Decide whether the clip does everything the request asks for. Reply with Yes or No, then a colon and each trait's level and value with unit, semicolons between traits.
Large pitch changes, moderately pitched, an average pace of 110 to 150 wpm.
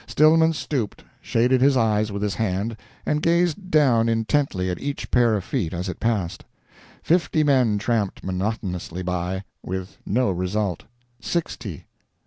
No: wide, 6.5 semitones; low, 110 Hz; average, 140 wpm